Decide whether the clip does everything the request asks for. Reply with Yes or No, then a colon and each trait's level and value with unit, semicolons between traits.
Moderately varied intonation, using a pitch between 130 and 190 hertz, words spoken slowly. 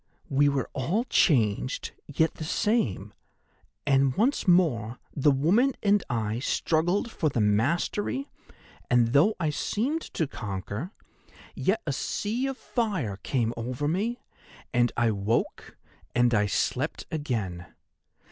No: wide, 8.6 semitones; medium, 140 Hz; slow, 130 wpm